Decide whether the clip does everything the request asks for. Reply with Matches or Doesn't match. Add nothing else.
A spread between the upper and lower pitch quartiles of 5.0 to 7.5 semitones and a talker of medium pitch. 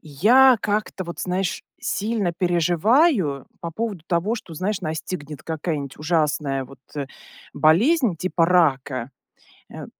Matches